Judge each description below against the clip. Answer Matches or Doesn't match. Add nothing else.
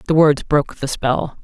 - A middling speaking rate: Doesn't match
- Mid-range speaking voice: Matches